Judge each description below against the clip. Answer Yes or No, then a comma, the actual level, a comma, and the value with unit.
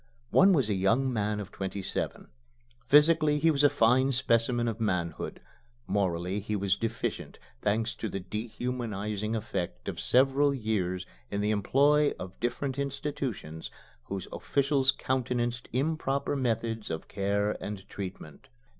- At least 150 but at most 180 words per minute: No, slow, 135 wpm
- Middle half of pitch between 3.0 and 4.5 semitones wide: No, average, 5.0 semitones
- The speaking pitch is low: Yes, low, 115 Hz